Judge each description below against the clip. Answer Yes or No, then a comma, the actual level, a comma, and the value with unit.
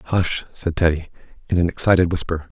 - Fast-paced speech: No, average, 160 wpm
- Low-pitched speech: Yes, very low, 85 Hz